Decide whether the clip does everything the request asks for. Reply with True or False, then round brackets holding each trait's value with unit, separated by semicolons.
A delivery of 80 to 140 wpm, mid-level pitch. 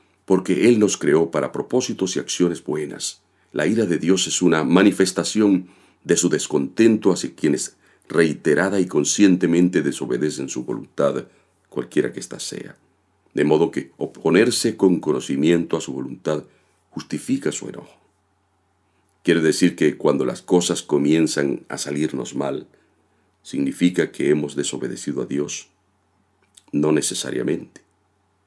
False (130 wpm; 95 Hz)